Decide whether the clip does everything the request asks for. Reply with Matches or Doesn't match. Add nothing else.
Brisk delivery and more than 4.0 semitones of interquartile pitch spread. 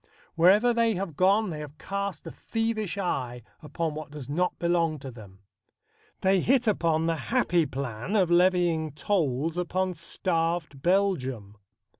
Doesn't match